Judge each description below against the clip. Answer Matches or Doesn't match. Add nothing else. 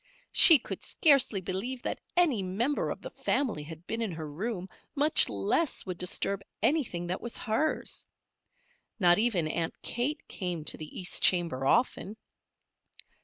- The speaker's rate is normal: Matches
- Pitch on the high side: Matches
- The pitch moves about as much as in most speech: Doesn't match